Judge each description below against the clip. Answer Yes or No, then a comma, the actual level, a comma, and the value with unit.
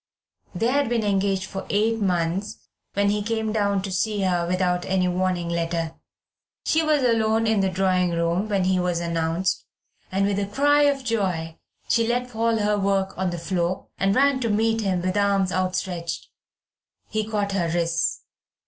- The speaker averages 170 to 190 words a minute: Yes, average, 175 wpm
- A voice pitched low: No, high, 195 Hz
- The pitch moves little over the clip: No, average, 3.4 semitones